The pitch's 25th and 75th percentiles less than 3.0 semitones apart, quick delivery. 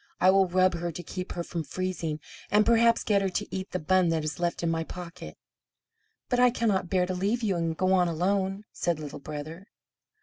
Yes: narrow, 2.6 semitones; fast, 215 wpm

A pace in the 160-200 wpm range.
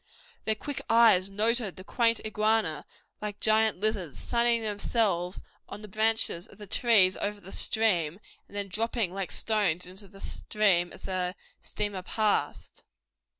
No: average, 150 wpm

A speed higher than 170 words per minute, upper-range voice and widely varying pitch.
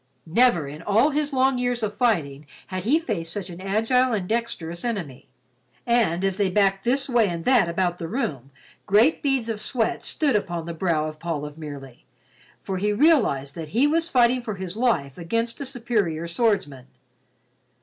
Yes: average, 180 wpm; high, 200 Hz; wide, 6.6 semitones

